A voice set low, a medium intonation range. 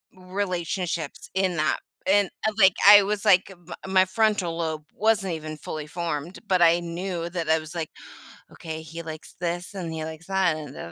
No: medium, 175 Hz; average, 3.0 semitones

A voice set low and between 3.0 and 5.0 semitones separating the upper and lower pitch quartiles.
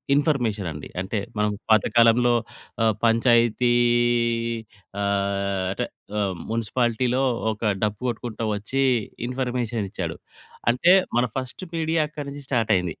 Yes: low, 115 Hz; average, 3.3 semitones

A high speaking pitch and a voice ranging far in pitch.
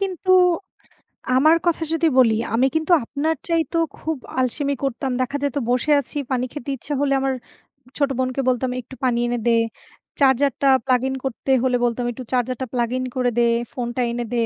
No: very high, 265 Hz; average, 2.7 semitones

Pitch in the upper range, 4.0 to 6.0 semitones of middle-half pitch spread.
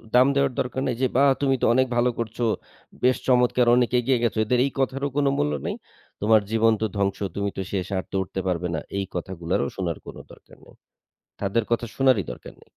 No: low, 115 Hz; average, 4.8 semitones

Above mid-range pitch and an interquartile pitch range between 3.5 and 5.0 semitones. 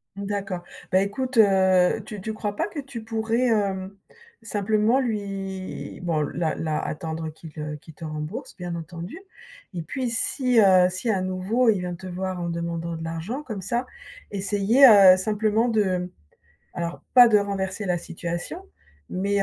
Yes: high, 195 Hz; average, 3.8 semitones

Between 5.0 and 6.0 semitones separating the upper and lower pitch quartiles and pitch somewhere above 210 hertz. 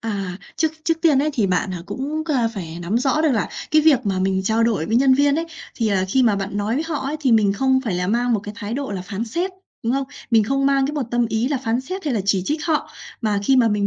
Yes: wide, 5.5 semitones; high, 235 Hz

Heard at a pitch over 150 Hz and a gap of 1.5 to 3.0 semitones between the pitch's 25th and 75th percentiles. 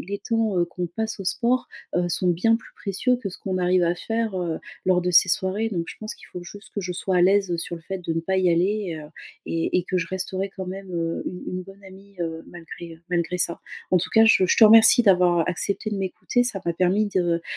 Yes: medium, 185 Hz; narrow, 2.5 semitones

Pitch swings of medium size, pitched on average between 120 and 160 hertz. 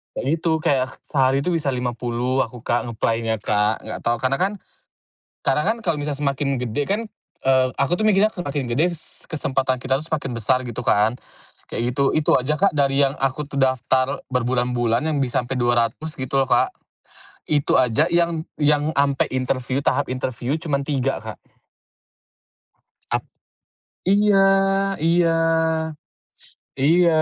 Yes: average, 3.4 semitones; low, 135 Hz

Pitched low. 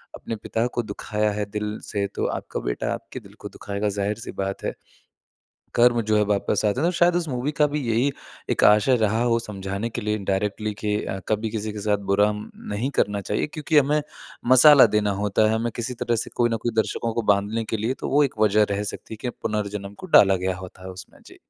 Yes: low, 105 Hz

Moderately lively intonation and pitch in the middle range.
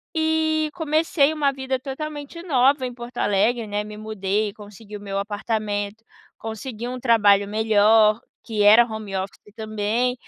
No: average, 4.1 semitones; high, 220 Hz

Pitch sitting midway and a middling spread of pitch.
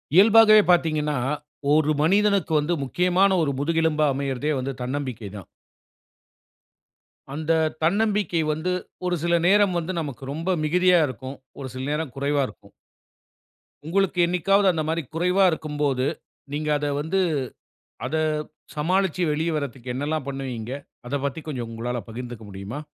Yes: medium, 155 Hz; average, 4.8 semitones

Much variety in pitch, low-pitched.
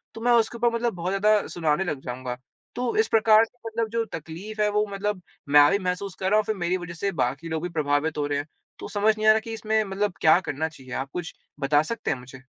No: wide, 6.1 semitones; high, 190 Hz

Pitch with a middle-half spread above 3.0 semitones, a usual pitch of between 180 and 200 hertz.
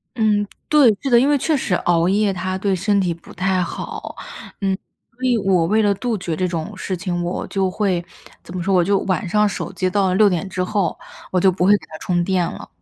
No: narrow, 2.5 semitones; high, 190 Hz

